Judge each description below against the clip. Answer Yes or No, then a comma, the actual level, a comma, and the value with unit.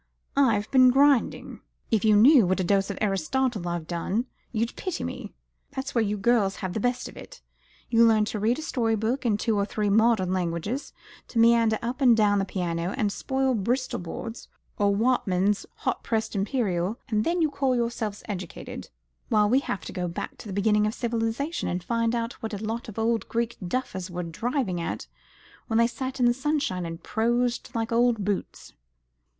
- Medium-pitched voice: No, high, 225 Hz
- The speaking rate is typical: Yes, average, 195 wpm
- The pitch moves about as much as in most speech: Yes, average, 3.5 semitones